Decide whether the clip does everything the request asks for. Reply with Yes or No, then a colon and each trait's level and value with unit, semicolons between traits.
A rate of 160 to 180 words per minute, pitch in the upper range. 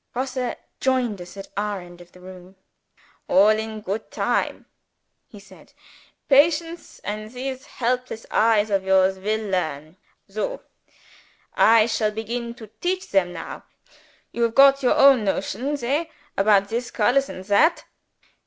No: average, 145 wpm; high, 220 Hz